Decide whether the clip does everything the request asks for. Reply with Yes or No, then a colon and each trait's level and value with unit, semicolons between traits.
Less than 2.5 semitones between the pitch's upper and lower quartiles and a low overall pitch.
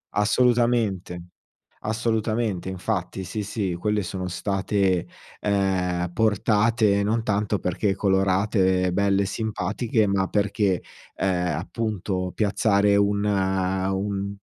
Yes: narrow, 2.1 semitones; low, 100 Hz